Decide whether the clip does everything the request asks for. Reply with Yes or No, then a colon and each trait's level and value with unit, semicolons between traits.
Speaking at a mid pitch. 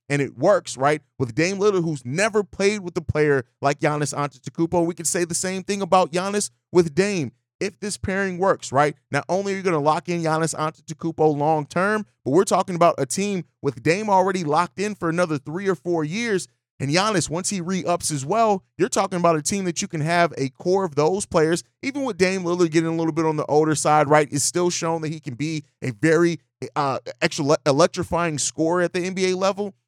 Yes: medium, 170 Hz